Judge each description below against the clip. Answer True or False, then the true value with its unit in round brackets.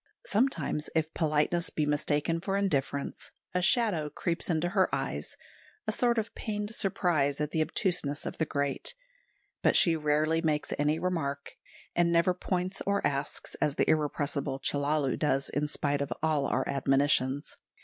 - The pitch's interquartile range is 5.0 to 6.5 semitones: False (3.9 semitones)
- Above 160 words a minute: False (155 wpm)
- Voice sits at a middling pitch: True (155 Hz)